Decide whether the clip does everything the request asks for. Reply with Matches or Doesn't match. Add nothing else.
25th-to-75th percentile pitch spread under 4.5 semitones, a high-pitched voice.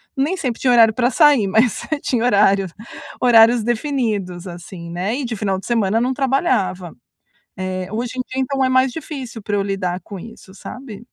Doesn't match